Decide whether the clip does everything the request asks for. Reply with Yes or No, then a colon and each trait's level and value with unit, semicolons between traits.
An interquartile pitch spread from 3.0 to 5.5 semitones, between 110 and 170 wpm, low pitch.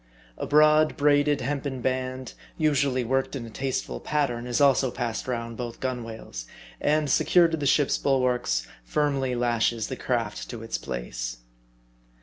Yes: average, 3.5 semitones; average, 145 wpm; low, 130 Hz